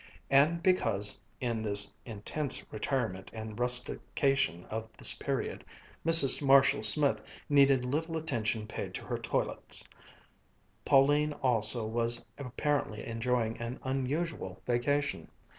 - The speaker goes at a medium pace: No, slow, 110 wpm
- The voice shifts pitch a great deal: No, average, 4.3 semitones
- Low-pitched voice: Yes, low, 125 Hz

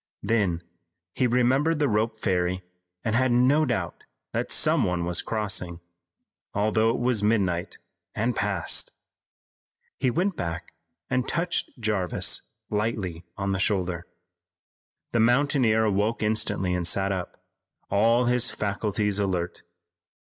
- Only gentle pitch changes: No, average, 4.4 semitones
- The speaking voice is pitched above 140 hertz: No, low, 105 Hz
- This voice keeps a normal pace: No, slow, 125 wpm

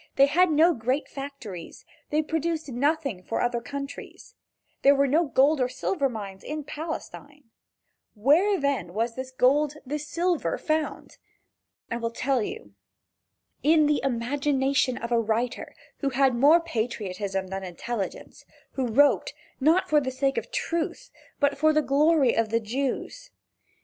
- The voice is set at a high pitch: Yes, very high, 275 Hz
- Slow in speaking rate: No, average, 150 wpm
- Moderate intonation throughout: Yes, average, 4.3 semitones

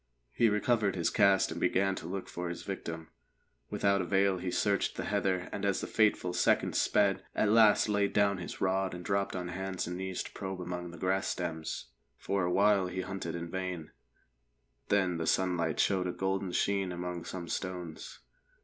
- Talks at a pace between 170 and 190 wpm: Yes, average, 185 wpm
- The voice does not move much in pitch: Yes, narrow, 1.9 semitones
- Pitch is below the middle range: Yes, very low, 95 Hz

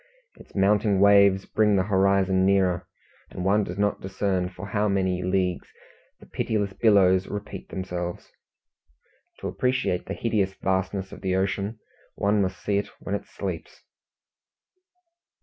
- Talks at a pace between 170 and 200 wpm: No, average, 140 wpm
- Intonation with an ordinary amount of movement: No, narrow, 1.5 semitones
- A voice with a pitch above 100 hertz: No, very low, 95 Hz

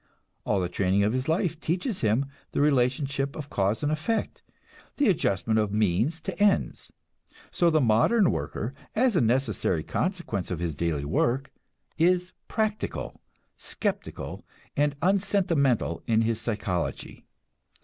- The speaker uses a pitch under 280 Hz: Yes, low, 135 Hz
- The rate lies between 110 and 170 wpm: Yes, slow, 135 wpm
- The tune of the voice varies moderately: No, wide, 8.6 semitones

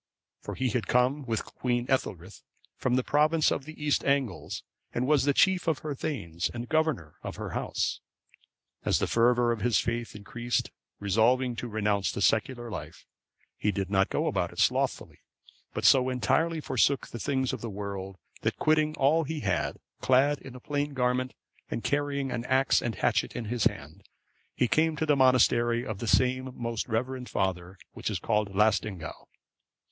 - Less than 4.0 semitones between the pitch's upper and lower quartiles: No, average, 4.4 semitones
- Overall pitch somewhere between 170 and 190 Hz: No, low, 125 Hz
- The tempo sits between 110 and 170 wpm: No, average, 180 wpm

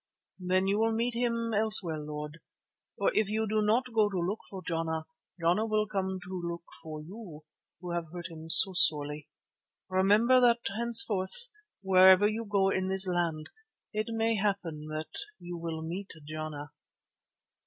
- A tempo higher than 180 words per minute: No, average, 165 wpm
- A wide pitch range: No, average, 4.6 semitones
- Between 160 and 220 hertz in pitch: Yes, high, 190 Hz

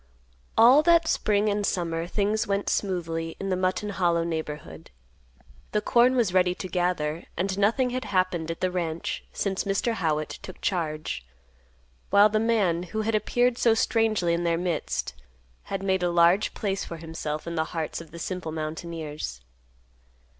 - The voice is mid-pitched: Yes, medium, 180 Hz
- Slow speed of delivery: No, average, 165 wpm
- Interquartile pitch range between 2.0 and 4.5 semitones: Yes, average, 4.0 semitones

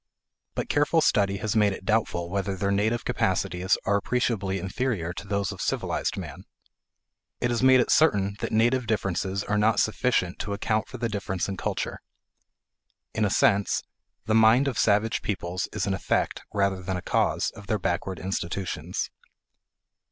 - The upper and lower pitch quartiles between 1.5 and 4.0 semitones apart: Yes, average, 2.8 semitones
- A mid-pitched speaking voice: No, low, 100 Hz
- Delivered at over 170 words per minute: No, average, 165 wpm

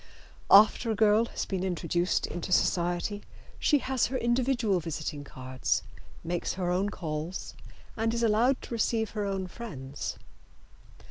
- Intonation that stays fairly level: No, average, 4.8 semitones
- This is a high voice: Yes, high, 200 Hz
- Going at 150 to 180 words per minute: No, average, 140 wpm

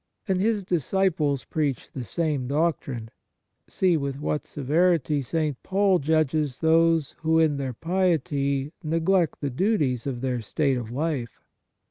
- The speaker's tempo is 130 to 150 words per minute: Yes, slow, 135 wpm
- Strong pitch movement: No, average, 3.6 semitones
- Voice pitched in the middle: Yes, medium, 155 Hz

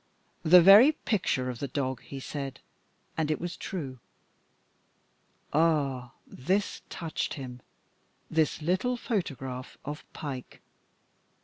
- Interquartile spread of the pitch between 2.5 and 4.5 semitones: No, average, 5.2 semitones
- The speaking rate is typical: No, slow, 110 wpm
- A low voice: No, medium, 150 Hz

